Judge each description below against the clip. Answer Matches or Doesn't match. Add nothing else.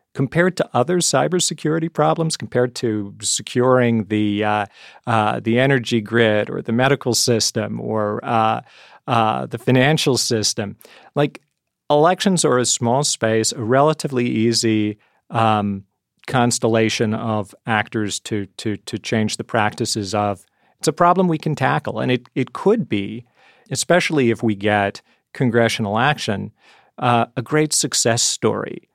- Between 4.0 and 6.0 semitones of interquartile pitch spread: Matches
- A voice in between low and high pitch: Doesn't match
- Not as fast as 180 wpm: Matches